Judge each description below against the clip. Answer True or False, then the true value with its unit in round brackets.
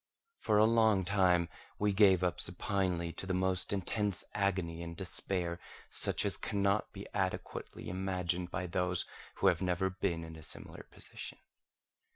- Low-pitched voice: True (95 Hz)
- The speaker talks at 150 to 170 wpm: True (155 wpm)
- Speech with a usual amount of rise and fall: False (2.0 semitones)